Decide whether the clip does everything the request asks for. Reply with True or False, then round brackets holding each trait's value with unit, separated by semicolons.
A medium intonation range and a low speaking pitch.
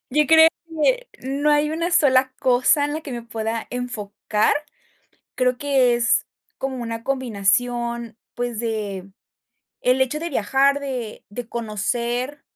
False (3.5 semitones; 250 Hz)